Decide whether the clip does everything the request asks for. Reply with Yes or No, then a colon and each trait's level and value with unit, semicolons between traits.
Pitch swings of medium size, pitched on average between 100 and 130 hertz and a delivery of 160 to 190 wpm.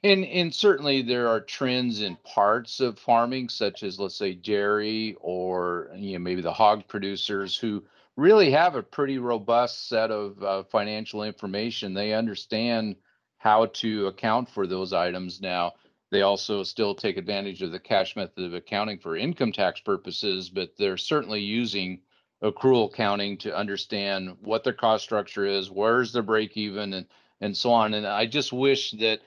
Yes: average, 3.2 semitones; low, 105 Hz; average, 170 wpm